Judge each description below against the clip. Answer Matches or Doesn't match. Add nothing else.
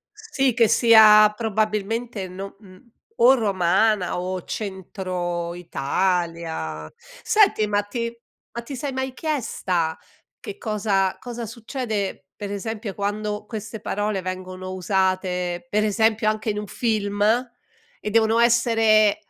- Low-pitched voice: Doesn't match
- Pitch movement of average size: Matches